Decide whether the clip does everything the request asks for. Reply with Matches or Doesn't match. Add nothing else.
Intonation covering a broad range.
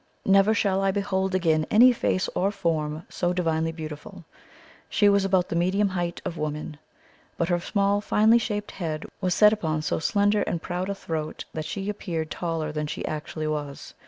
Doesn't match